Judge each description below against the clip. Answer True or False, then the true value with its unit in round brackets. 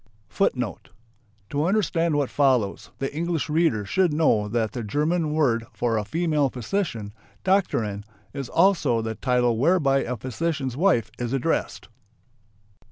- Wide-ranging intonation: True (6.0 semitones)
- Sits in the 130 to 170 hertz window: True (140 Hz)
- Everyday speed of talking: False (130 wpm)